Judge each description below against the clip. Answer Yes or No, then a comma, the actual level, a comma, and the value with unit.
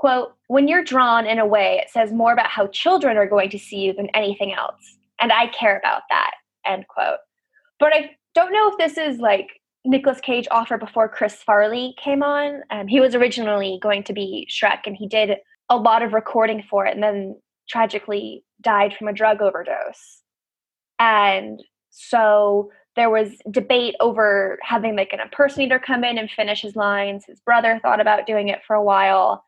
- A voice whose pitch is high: Yes, high, 225 Hz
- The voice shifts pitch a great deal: No, average, 4.1 semitones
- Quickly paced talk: No, average, 190 wpm